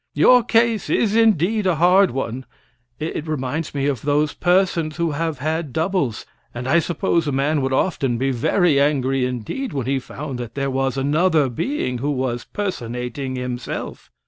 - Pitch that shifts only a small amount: No, average, 4.7 semitones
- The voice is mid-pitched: Yes, medium, 145 Hz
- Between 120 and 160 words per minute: No, average, 170 wpm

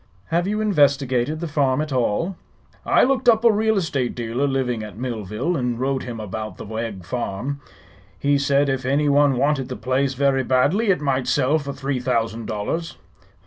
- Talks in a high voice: No, low, 135 Hz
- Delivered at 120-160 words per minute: No, average, 185 wpm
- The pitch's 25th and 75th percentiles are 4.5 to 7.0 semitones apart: No, average, 3.4 semitones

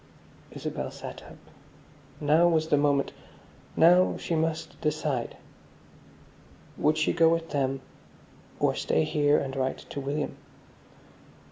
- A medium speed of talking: No, slow, 120 wpm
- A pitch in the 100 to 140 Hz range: No, medium, 150 Hz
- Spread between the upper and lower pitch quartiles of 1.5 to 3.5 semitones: Yes, narrow, 2.5 semitones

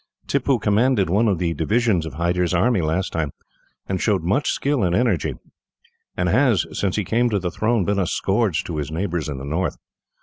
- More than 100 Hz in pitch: No, very low, 95 Hz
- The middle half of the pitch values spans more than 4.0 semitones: Yes, average, 5.1 semitones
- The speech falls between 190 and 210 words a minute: Yes, average, 200 wpm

